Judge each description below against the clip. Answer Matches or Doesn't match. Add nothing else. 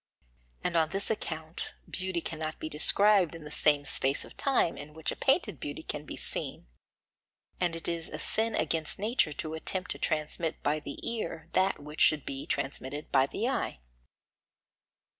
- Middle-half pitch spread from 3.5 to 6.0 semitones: Doesn't match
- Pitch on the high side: Doesn't match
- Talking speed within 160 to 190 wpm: Matches